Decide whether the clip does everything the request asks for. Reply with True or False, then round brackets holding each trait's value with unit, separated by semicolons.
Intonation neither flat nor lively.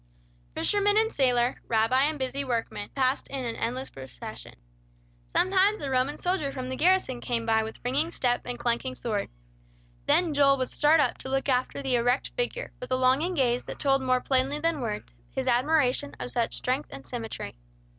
True (3.4 semitones)